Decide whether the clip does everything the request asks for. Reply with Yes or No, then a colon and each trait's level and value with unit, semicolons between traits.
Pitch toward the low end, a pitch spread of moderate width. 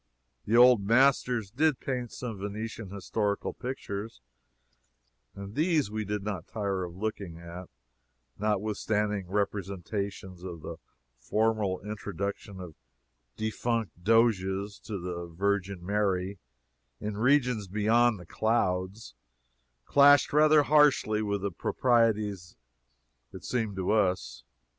Yes: low, 105 Hz; average, 3.0 semitones